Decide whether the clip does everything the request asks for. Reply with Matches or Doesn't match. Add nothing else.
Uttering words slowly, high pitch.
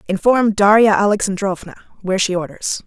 Matches